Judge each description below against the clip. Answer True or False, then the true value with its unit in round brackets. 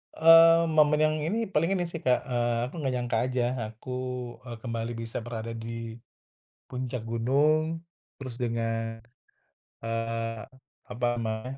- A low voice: True (120 Hz)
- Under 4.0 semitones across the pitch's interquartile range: False (4.8 semitones)